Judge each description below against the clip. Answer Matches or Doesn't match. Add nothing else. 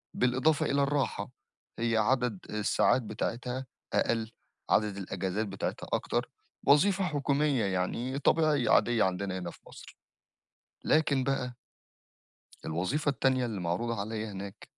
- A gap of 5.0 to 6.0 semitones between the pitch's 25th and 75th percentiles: Matches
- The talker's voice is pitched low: Matches